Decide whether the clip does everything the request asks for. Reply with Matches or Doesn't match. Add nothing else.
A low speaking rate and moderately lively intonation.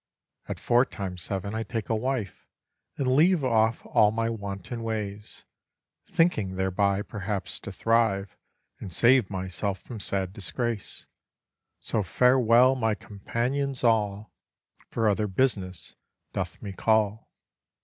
Matches